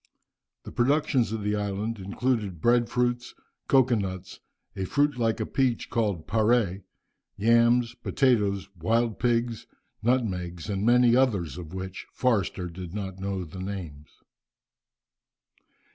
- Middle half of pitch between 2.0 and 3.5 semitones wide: No, average, 4.2 semitones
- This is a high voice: No, low, 110 Hz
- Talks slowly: Yes, slow, 125 wpm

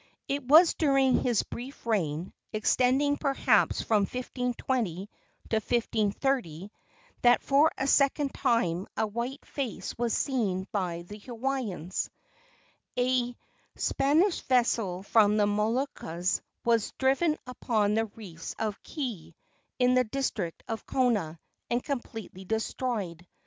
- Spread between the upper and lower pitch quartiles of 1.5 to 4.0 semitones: No, average, 4.7 semitones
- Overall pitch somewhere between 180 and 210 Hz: No, high, 235 Hz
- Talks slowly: Yes, slow, 120 wpm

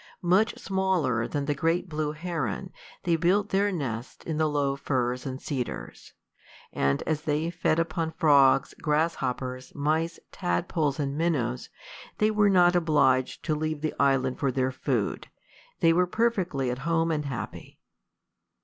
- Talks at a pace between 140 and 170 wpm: Yes, average, 150 wpm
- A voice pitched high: No, medium, 150 Hz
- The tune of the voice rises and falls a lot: No, average, 4.0 semitones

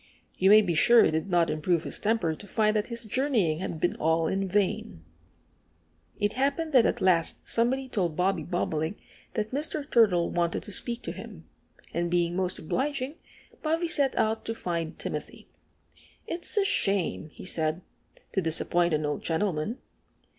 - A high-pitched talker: Yes, high, 195 Hz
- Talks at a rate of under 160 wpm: No, average, 170 wpm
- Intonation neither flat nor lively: No, wide, 5.8 semitones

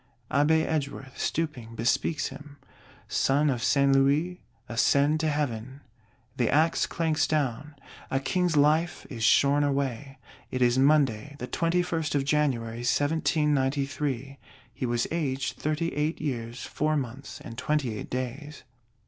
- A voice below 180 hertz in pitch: Yes, medium, 140 Hz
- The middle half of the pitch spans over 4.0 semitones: No, average, 2.9 semitones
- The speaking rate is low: Yes, slow, 130 wpm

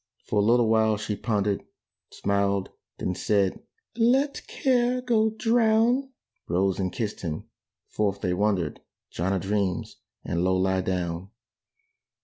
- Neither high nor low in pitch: No, low, 100 Hz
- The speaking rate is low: Yes, slow, 130 wpm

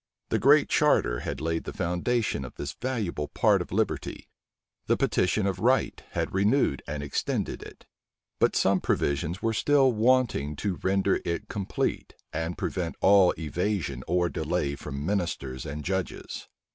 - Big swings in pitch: Yes, wide, 6.0 semitones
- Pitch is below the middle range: Yes, very low, 90 Hz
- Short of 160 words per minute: Yes, average, 150 wpm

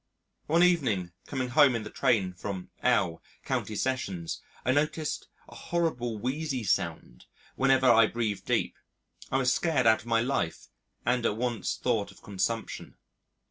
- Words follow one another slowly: No, average, 150 wpm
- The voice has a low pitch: Yes, low, 120 Hz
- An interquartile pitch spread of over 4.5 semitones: No, average, 4.1 semitones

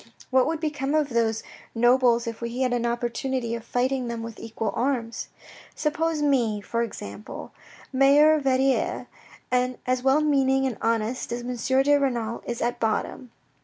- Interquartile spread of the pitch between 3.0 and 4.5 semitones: No, narrow, 2.6 semitones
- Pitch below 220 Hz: No, very high, 250 Hz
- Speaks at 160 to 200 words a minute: Yes, average, 165 wpm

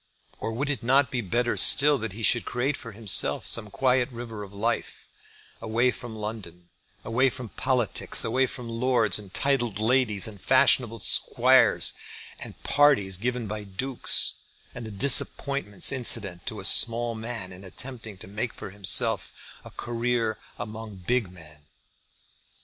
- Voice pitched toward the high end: No, low, 115 Hz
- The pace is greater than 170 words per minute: No, average, 155 wpm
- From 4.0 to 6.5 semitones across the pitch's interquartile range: No, average, 3.4 semitones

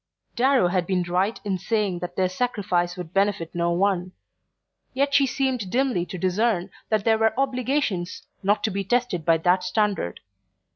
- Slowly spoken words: No, average, 165 wpm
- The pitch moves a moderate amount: Yes, average, 4.7 semitones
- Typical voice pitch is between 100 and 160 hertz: No, high, 195 Hz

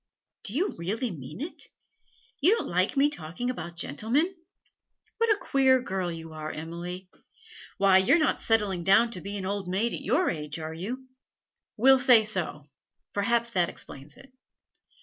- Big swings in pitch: Yes, wide, 6.8 semitones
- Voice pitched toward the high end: Yes, high, 200 Hz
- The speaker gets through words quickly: No, average, 170 wpm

